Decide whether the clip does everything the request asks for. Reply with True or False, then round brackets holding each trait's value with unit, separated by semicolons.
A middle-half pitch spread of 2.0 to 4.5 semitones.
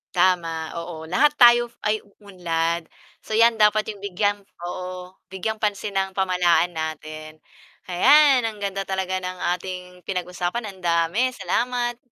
True (3.4 semitones)